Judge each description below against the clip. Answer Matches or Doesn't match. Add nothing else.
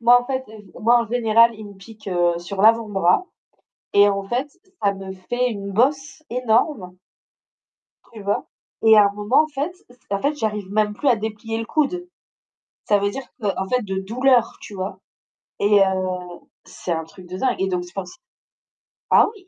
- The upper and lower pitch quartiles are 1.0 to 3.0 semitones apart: Doesn't match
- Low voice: Doesn't match